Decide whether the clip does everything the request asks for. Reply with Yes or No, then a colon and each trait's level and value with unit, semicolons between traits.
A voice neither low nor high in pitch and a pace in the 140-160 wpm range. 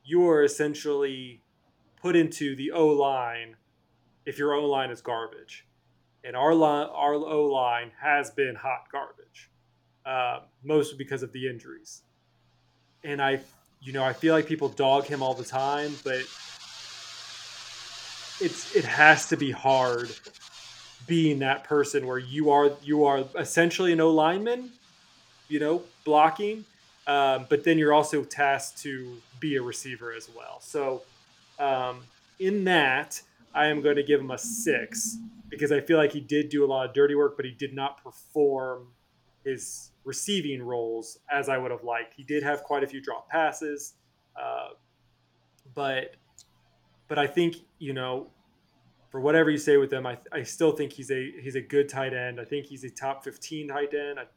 No: medium, 145 Hz; average, 170 wpm